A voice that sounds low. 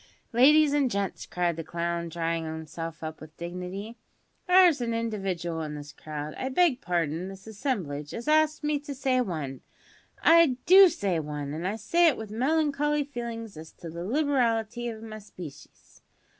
No: high, 210 Hz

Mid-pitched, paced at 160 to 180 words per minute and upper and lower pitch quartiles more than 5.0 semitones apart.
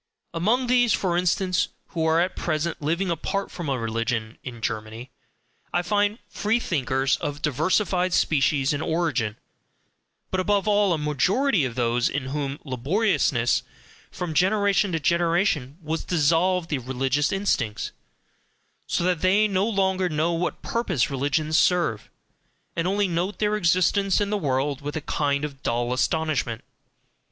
No: medium, 165 Hz; average, 145 wpm; wide, 5.5 semitones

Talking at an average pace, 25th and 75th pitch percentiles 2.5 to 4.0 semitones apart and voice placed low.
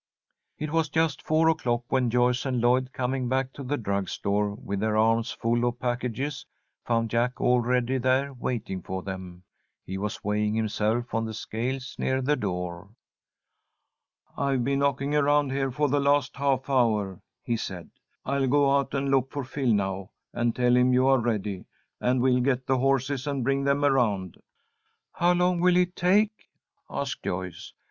Yes: average, 170 wpm; average, 3.7 semitones; low, 125 Hz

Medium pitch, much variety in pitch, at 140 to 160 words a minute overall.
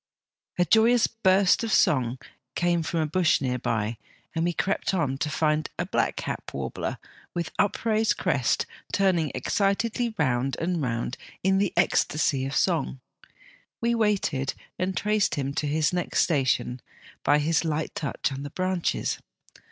Yes: medium, 165 Hz; wide, 5.7 semitones; average, 150 wpm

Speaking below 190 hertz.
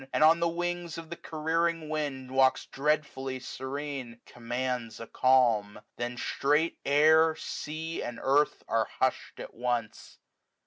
Yes: medium, 140 Hz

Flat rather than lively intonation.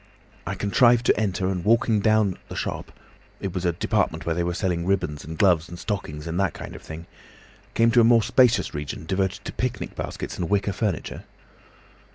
No: average, 4.2 semitones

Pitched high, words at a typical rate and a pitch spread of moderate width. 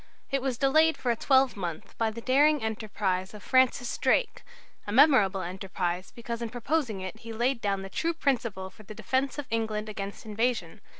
Yes: high, 225 Hz; average, 180 wpm; average, 4.7 semitones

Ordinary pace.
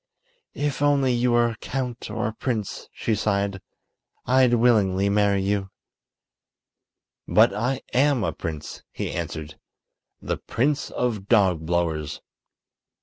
No: slow, 120 wpm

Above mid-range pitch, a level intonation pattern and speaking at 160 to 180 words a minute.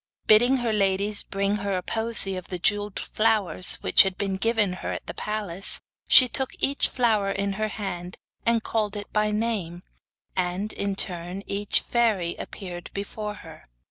Yes: high, 205 Hz; narrow, 2.2 semitones; average, 165 wpm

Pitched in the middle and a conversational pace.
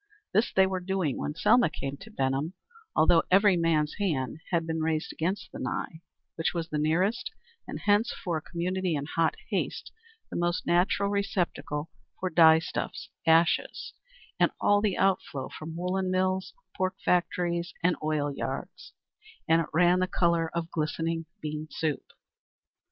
Yes: medium, 170 Hz; average, 155 wpm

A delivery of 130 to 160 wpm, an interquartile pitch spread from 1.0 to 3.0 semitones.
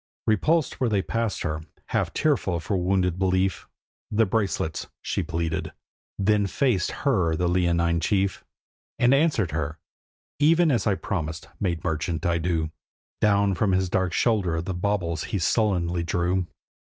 No: average, 145 wpm; average, 3.8 semitones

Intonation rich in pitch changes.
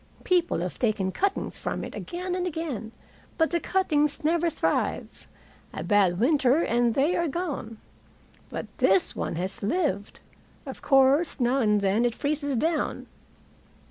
Yes: wide, 7.2 semitones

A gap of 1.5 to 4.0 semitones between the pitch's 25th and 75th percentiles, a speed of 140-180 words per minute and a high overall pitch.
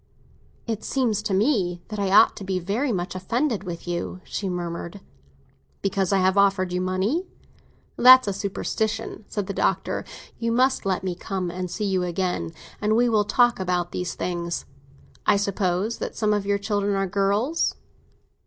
Yes: average, 3.0 semitones; average, 170 wpm; high, 195 Hz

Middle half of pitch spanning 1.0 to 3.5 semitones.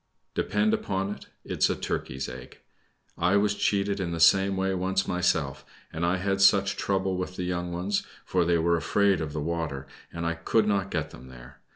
Yes: average, 2.8 semitones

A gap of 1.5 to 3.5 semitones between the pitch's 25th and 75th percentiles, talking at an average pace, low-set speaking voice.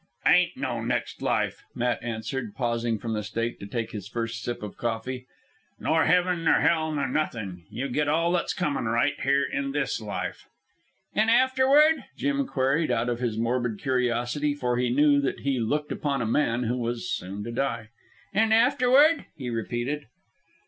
No: average, 4.5 semitones; average, 175 wpm; low, 125 Hz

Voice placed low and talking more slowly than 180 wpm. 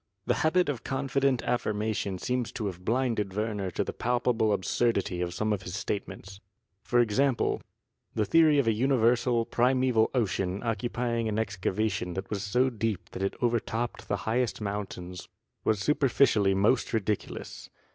Yes: low, 110 Hz; average, 150 wpm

